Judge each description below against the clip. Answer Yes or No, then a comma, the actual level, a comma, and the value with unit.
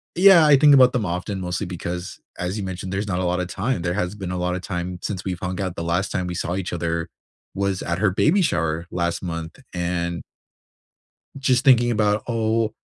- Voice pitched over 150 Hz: No, very low, 90 Hz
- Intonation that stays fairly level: No, average, 3.5 semitones